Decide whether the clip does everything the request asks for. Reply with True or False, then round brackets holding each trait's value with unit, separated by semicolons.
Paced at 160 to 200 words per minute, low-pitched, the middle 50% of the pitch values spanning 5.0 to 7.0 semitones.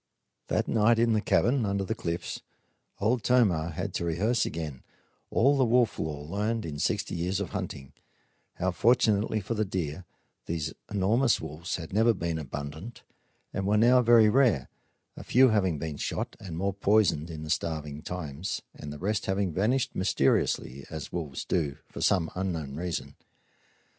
True (165 wpm; 95 Hz; 5.5 semitones)